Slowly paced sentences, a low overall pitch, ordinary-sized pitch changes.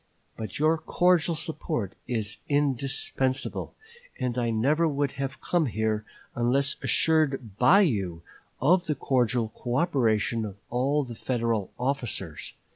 Yes: slow, 120 wpm; low, 130 Hz; average, 4.7 semitones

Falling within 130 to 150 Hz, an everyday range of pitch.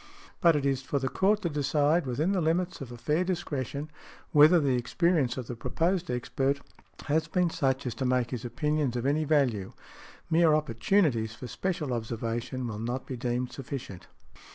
Yes: medium, 140 Hz; average, 4.6 semitones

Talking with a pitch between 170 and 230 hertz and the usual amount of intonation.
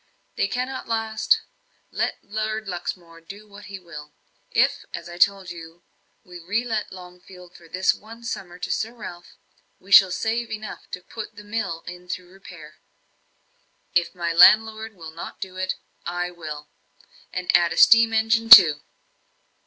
Yes: medium, 185 Hz; average, 3.9 semitones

